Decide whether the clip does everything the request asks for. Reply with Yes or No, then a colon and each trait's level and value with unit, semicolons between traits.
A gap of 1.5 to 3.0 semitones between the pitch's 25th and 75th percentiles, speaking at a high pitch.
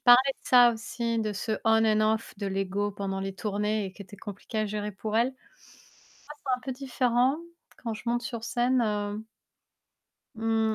Yes: average, 2.7 semitones; high, 220 Hz